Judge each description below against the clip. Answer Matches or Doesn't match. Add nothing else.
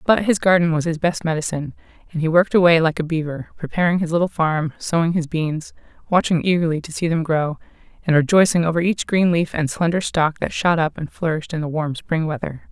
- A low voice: Doesn't match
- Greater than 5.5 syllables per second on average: Matches